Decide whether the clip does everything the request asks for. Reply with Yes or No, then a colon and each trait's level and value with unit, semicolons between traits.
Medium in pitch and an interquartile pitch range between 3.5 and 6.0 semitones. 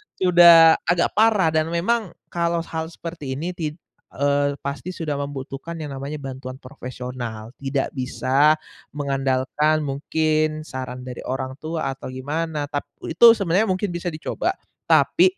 Yes: medium, 150 Hz; average, 3.8 semitones